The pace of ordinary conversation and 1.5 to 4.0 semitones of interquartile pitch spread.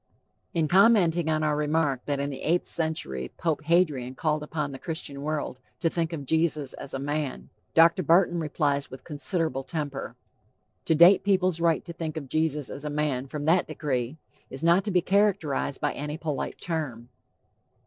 Yes: average, 180 wpm; average, 3.0 semitones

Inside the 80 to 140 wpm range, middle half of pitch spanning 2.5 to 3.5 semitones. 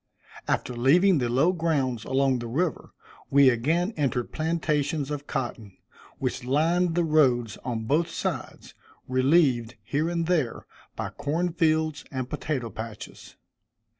No: slow, 135 wpm; average, 4.7 semitones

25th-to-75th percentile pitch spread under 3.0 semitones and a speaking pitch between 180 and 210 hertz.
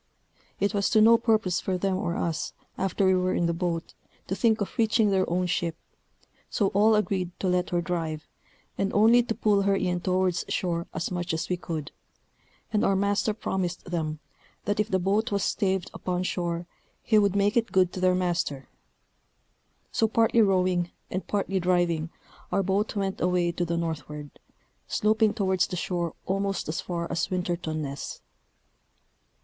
Yes: narrow, 2.6 semitones; medium, 185 Hz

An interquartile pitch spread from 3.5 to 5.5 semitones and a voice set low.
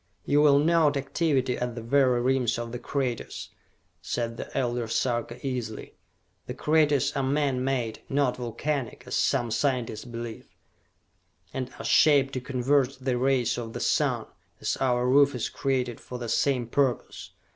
No: narrow, 2.4 semitones; low, 130 Hz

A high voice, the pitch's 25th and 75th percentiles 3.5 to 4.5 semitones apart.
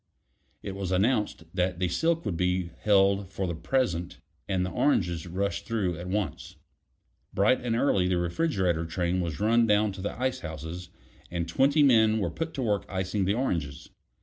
No: very low, 95 Hz; average, 4.0 semitones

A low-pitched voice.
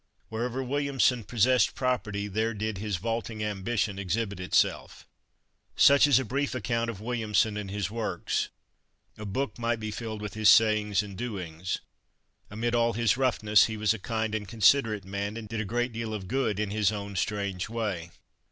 Yes: low, 110 Hz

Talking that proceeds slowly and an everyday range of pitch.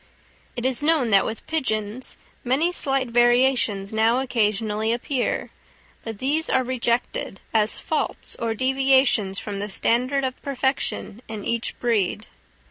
Yes: slow, 130 wpm; average, 3.4 semitones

